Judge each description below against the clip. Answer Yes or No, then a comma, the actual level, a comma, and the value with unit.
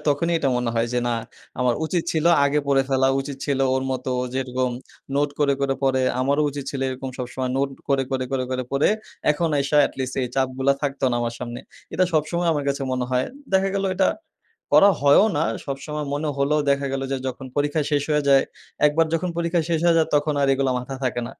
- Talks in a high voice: No, medium, 140 Hz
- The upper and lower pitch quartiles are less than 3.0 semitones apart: Yes, narrow, 2.4 semitones